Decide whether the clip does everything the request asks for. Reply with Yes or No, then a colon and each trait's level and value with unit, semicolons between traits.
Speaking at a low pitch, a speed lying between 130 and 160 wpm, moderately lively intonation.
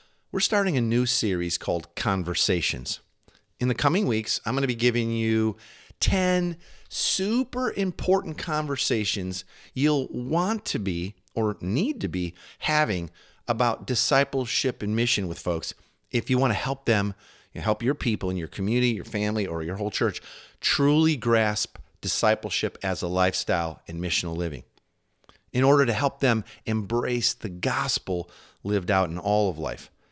No: low, 110 Hz; average, 155 wpm; wide, 5.9 semitones